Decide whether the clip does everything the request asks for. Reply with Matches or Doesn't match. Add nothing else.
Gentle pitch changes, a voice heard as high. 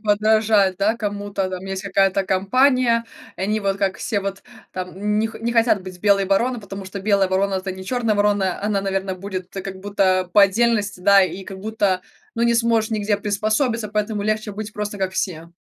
Matches